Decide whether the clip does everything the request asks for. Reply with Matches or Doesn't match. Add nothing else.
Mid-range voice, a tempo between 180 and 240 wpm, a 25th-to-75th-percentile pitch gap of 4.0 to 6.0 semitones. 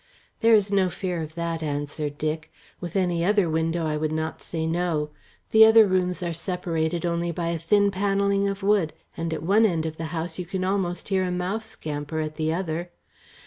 Doesn't match